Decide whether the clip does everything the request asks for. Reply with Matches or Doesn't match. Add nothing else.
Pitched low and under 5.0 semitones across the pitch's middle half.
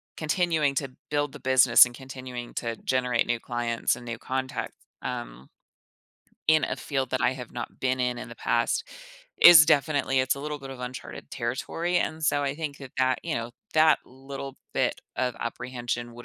Matches